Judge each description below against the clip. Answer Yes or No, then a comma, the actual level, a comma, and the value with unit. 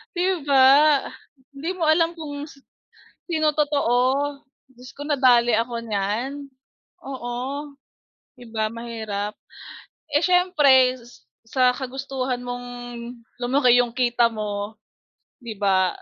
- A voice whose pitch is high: Yes, very high, 255 Hz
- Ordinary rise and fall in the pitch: Yes, average, 3.5 semitones